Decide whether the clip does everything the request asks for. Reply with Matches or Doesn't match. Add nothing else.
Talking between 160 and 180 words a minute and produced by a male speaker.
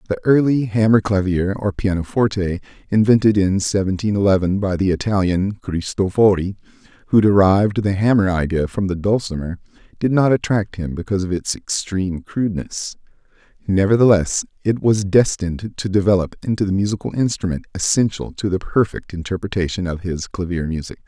Doesn't match